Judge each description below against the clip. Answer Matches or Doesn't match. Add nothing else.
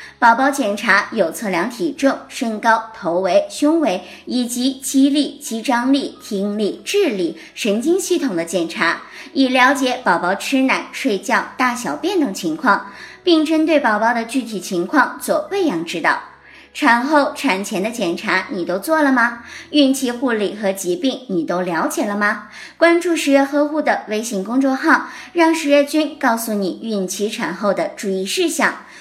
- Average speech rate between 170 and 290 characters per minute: Matches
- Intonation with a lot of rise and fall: Matches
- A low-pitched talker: Doesn't match